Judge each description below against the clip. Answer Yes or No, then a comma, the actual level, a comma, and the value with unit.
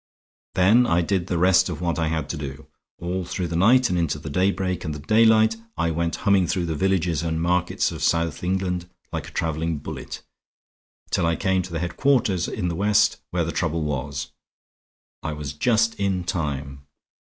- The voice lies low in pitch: Yes, very low, 85 Hz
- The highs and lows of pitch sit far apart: No, average, 2.9 semitones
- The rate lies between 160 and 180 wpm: No, average, 190 wpm